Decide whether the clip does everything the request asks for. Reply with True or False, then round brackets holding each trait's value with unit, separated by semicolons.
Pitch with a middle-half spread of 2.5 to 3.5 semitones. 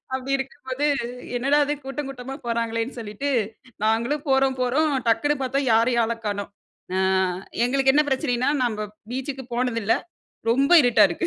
True (2.8 semitones)